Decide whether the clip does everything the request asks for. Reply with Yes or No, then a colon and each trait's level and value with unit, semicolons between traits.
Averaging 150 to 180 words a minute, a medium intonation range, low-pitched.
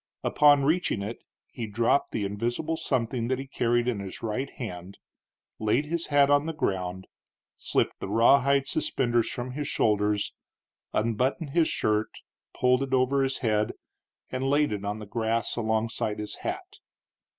Yes: average, 155 wpm; average, 4.5 semitones; low, 120 Hz